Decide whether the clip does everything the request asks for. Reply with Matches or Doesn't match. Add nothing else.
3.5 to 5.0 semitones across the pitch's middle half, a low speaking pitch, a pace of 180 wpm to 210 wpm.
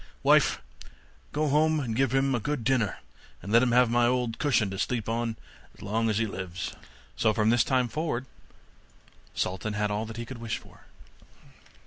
Doesn't match